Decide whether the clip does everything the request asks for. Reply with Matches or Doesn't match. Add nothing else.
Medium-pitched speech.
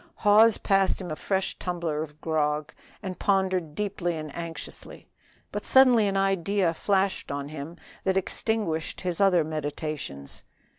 Matches